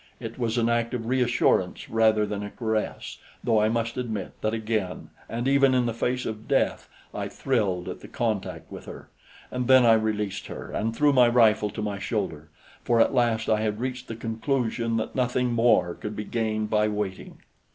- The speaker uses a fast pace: No, average, 195 wpm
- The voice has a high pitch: No, low, 115 Hz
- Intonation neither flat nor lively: No, narrow, 2.2 semitones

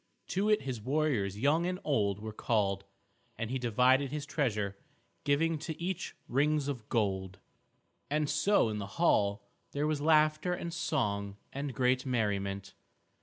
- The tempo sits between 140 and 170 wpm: Yes, average, 150 wpm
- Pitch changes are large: Yes, wide, 6.5 semitones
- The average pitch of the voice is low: Yes, low, 130 Hz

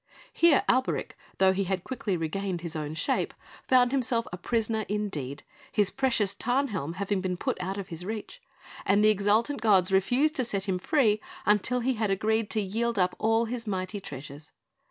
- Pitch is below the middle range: No, high, 205 Hz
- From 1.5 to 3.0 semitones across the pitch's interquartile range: No, average, 3.8 semitones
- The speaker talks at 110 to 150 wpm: No, average, 180 wpm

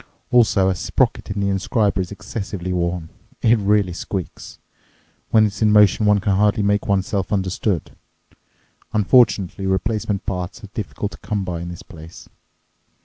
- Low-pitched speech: Yes, low, 100 Hz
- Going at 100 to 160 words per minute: Yes, average, 150 wpm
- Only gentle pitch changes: Yes, narrow, 2.2 semitones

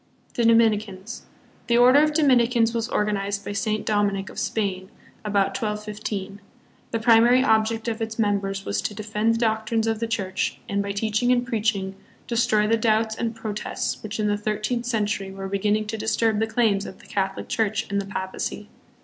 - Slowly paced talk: No, average, 190 wpm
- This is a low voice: No, high, 215 Hz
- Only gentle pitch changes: Yes, narrow, 2.1 semitones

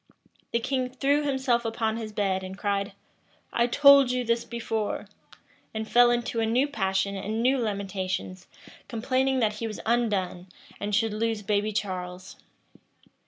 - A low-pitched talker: No, high, 225 Hz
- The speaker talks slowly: No, average, 150 wpm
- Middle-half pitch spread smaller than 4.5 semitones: Yes, average, 3.3 semitones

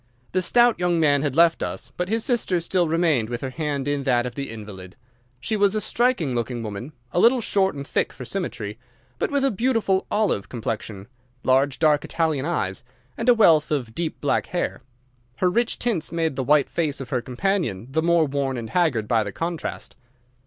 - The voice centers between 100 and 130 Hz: No, medium, 155 Hz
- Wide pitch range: Yes, wide, 6.5 semitones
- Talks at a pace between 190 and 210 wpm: Yes, average, 200 wpm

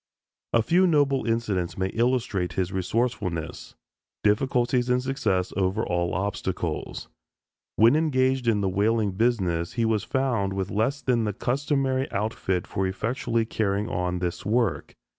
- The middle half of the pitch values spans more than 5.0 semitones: No, average, 4.7 semitones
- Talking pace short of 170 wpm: Yes, average, 140 wpm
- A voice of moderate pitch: No, low, 110 Hz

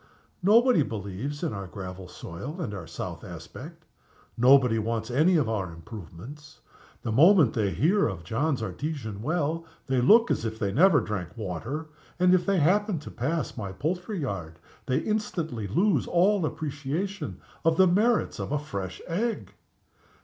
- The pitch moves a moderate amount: No, wide, 8.5 semitones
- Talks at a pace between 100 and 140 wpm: No, average, 155 wpm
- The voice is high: No, medium, 140 Hz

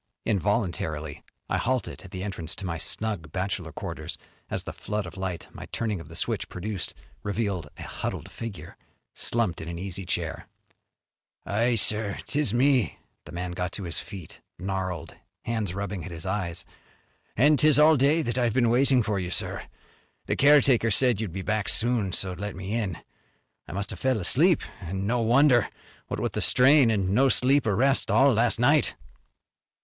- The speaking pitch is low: Yes, low, 105 Hz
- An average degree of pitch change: Yes, average, 5.0 semitones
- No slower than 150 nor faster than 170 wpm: No, average, 180 wpm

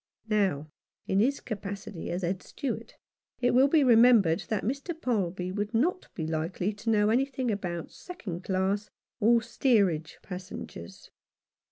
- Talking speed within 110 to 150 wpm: Yes, average, 140 wpm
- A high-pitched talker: Yes, high, 205 Hz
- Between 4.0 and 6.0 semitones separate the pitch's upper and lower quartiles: Yes, average, 5.0 semitones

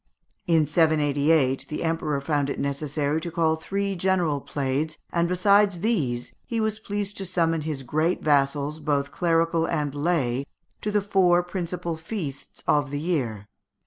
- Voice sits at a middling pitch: Yes, medium, 160 Hz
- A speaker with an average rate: Yes, average, 150 wpm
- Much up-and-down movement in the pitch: No, average, 3.6 semitones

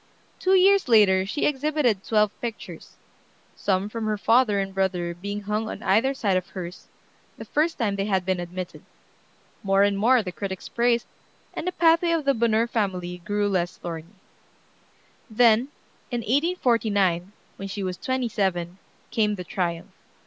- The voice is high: Yes, high, 205 Hz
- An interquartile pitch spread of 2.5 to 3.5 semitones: No, average, 4.1 semitones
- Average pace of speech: Yes, average, 160 wpm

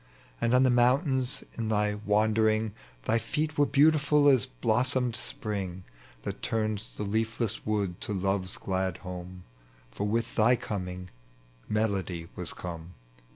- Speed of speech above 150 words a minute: No, average, 140 wpm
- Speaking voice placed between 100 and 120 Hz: Yes, low, 110 Hz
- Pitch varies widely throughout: No, average, 4.2 semitones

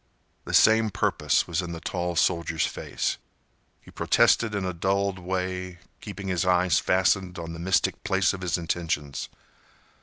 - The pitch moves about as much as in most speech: No, narrow, 1.8 semitones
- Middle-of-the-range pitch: No, very low, 90 Hz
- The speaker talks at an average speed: Yes, average, 155 wpm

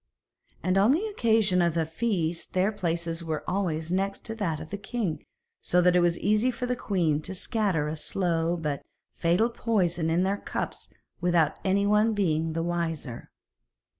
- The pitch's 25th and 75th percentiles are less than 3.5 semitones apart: No, average, 3.8 semitones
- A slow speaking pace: No, average, 165 wpm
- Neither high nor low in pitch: Yes, medium, 180 Hz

